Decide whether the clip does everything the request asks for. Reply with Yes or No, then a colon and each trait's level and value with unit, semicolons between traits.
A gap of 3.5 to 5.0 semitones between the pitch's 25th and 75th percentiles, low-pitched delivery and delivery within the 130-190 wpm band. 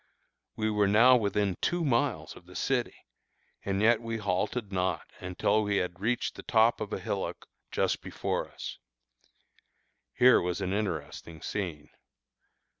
Yes: average, 4.1 semitones; low, 105 Hz; average, 145 wpm